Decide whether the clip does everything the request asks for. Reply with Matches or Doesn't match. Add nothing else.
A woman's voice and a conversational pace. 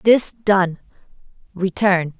Doesn't match